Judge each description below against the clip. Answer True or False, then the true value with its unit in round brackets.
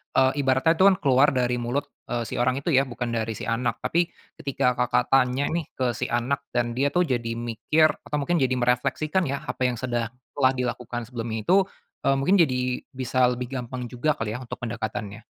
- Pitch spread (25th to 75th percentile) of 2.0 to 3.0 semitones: True (2.4 semitones)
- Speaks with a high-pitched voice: False (125 Hz)